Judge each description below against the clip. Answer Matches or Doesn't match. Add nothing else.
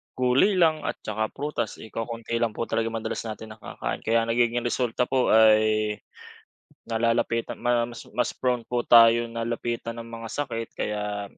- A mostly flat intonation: Matches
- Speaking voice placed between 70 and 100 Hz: Doesn't match